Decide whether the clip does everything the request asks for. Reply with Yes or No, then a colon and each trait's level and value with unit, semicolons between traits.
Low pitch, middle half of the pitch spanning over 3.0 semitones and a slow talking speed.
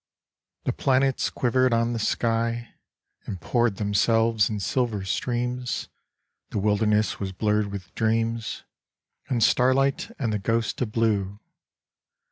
No: low, 115 Hz; narrow, 2.4 semitones; slow, 120 wpm